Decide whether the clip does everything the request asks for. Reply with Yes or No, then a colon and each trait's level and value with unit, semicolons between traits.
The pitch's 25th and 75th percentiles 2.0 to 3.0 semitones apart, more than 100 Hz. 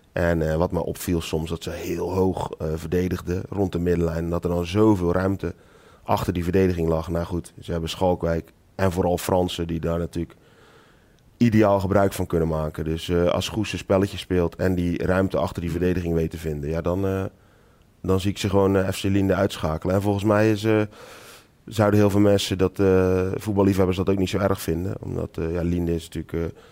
No: narrow, 2.6 semitones; very low, 90 Hz